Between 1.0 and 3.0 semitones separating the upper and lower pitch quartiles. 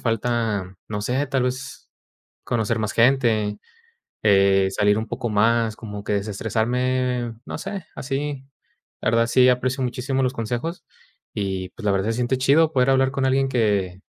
No: average, 3.8 semitones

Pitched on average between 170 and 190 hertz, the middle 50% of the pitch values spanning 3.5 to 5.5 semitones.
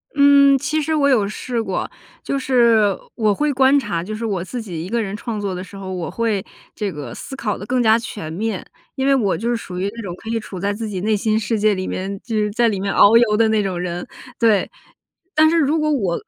No: high, 215 Hz; average, 3.8 semitones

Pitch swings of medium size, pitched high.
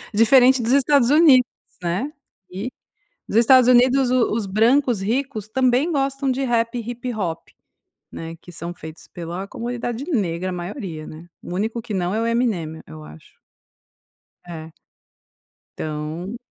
No: wide, 6.4 semitones; high, 230 Hz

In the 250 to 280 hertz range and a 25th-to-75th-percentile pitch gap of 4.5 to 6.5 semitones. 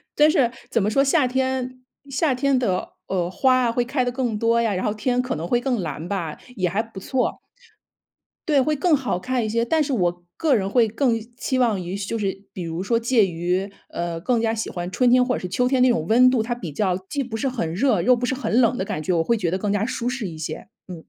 No: high, 230 Hz; average, 5.2 semitones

